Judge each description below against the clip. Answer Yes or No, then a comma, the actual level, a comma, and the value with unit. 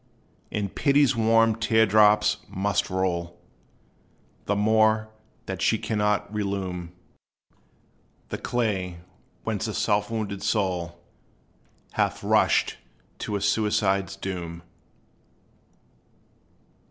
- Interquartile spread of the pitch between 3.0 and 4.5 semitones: No, narrow, 2.5 semitones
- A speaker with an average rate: No, slow, 90 wpm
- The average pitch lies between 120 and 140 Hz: No, low, 105 Hz